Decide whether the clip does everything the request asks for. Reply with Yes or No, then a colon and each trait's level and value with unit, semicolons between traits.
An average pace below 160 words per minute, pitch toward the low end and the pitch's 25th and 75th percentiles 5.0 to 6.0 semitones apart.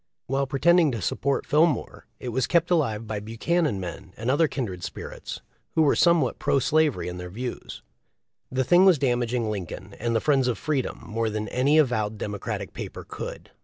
No: average, 180 wpm; low, 125 Hz; wide, 5.6 semitones